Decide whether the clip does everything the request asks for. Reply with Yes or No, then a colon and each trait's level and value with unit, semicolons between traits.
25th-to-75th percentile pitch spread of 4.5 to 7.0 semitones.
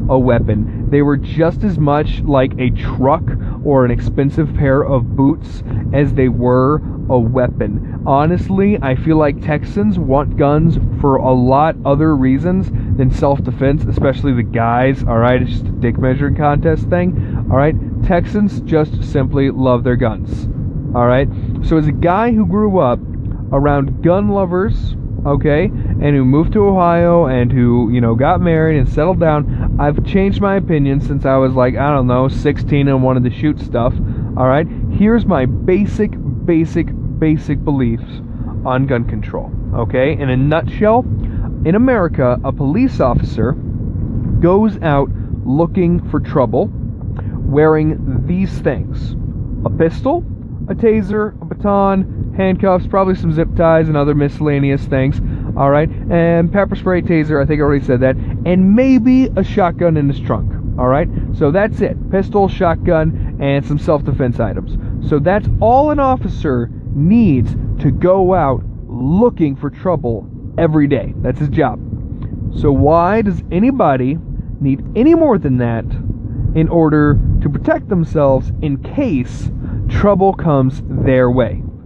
Yes: average, 5.0 semitones